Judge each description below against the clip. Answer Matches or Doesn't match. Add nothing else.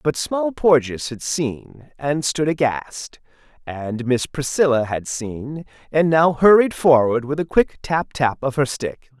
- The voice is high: Doesn't match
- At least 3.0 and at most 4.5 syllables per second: Matches